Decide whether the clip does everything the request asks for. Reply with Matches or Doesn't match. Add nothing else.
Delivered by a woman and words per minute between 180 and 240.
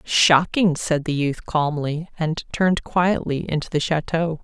Doesn't match